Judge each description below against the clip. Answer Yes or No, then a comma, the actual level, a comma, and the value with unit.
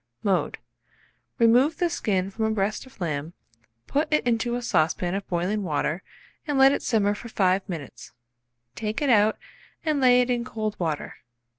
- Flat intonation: No, average, 5.0 semitones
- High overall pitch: Yes, high, 215 Hz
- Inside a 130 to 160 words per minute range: No, average, 170 wpm